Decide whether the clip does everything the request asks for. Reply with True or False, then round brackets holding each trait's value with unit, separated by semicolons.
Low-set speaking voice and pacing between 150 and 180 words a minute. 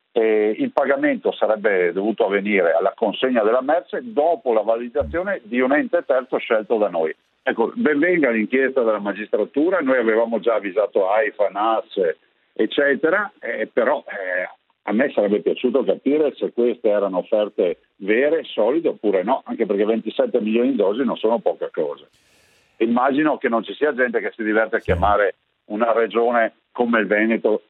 True (120 Hz; 160 wpm)